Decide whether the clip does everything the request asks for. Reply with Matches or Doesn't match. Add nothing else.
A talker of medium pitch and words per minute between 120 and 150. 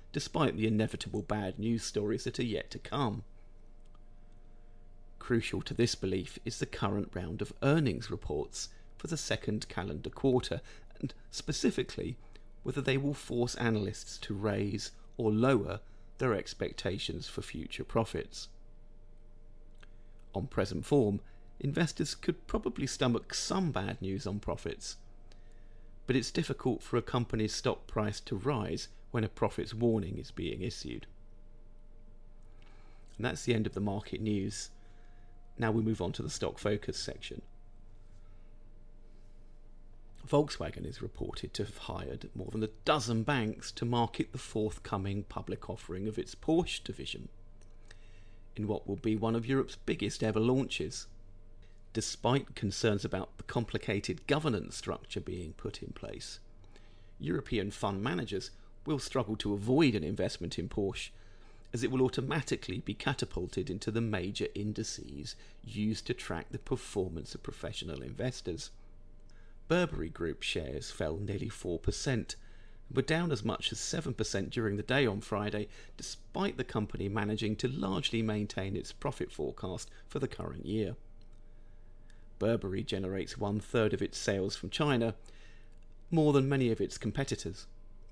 Doesn't match